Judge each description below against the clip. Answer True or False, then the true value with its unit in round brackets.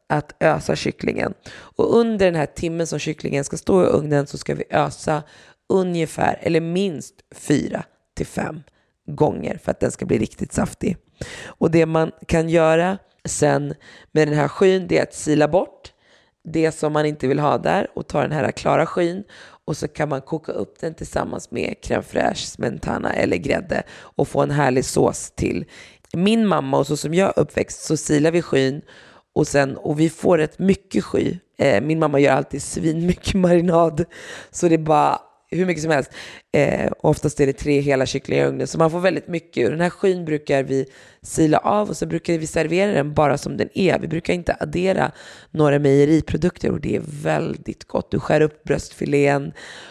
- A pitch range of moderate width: True (3.2 semitones)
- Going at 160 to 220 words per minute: True (190 wpm)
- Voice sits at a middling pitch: True (160 Hz)